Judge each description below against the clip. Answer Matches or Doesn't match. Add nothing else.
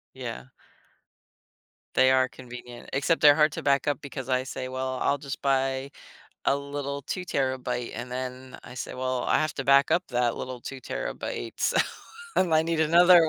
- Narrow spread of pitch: Matches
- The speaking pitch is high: Doesn't match